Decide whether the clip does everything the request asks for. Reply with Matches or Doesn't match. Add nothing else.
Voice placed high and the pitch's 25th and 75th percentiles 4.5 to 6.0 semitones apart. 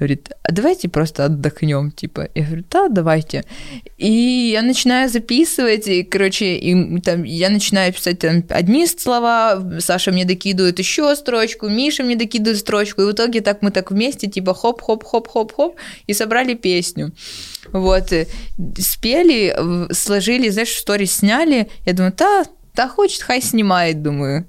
Matches